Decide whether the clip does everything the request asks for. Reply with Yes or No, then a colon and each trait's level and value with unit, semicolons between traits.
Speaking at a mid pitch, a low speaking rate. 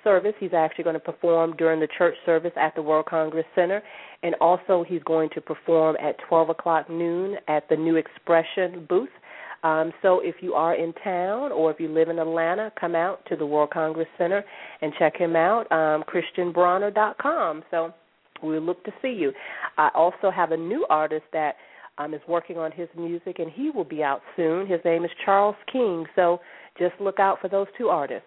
No: medium, 170 Hz; average, 200 wpm